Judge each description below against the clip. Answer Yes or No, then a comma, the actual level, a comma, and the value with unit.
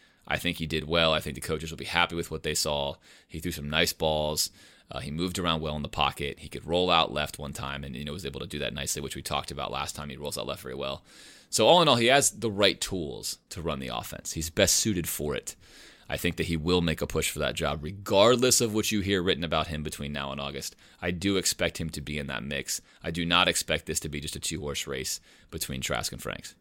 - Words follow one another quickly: Yes, fast, 275 wpm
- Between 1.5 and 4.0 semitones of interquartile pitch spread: Yes, average, 2.9 semitones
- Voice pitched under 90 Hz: Yes, very low, 80 Hz